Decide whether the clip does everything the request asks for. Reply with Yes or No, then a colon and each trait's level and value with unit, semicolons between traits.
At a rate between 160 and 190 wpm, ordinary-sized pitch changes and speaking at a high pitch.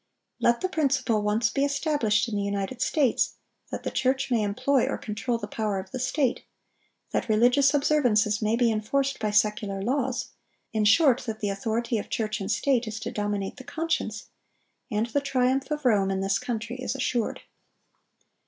Yes: average, 180 wpm; average, 4.1 semitones; high, 235 Hz